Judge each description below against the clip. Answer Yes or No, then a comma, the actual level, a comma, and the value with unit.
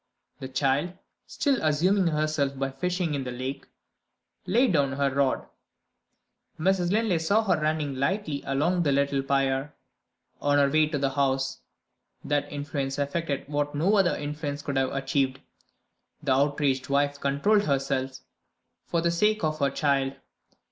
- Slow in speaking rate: No, average, 150 wpm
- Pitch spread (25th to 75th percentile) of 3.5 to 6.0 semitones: No, average, 3.0 semitones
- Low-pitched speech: No, medium, 145 Hz